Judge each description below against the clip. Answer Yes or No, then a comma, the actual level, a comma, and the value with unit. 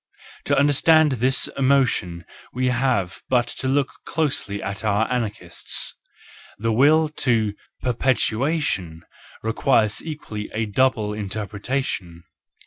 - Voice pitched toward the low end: Yes, low, 115 Hz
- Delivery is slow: Yes, slow, 110 wpm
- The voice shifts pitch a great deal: No, average, 4.6 semitones